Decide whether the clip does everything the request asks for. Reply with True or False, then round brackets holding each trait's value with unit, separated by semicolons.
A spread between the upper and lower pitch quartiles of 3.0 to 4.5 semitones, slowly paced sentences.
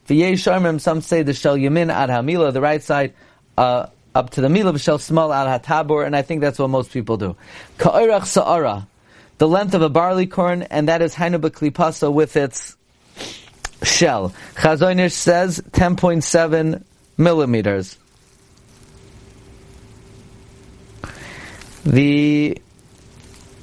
True (3.9 semitones; 130 wpm)